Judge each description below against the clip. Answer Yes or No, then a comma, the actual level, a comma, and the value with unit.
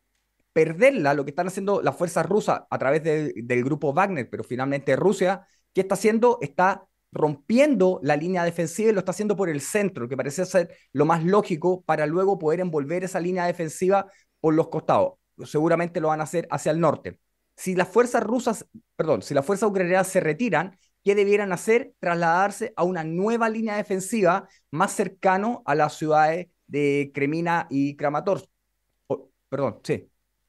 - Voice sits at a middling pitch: Yes, medium, 180 Hz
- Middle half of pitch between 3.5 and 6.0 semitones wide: Yes, average, 4.3 semitones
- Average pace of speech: Yes, average, 175 wpm